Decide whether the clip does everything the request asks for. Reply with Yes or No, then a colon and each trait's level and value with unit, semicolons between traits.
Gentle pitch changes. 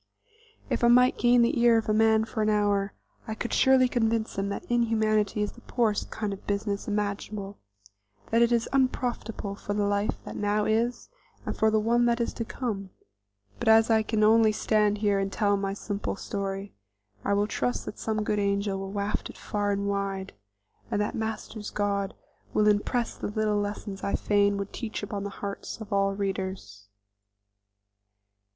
Yes: narrow, 1.8 semitones